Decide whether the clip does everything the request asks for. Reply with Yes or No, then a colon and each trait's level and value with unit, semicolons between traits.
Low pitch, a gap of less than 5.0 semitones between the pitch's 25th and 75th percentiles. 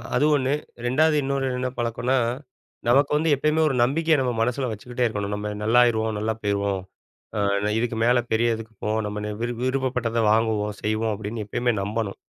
Yes: low, 115 Hz; average, 3.2 semitones